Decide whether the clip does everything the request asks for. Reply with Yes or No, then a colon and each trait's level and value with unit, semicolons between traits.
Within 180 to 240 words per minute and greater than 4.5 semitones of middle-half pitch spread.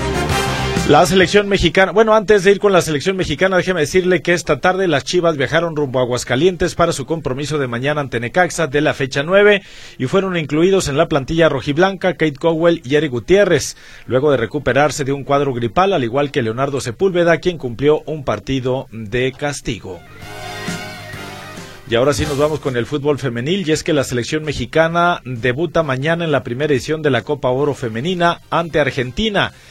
Yes: average, 185 wpm; average, 4.9 semitones